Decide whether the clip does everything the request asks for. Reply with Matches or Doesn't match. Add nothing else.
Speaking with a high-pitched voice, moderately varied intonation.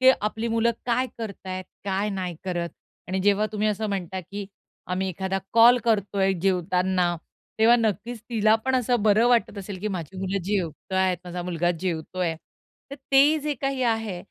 Matches